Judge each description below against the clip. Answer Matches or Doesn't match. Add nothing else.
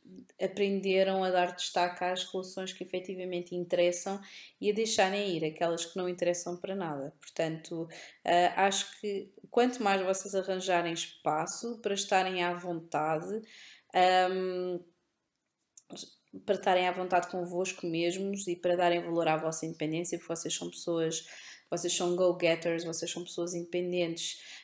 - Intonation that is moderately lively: Doesn't match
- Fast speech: Doesn't match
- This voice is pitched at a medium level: Matches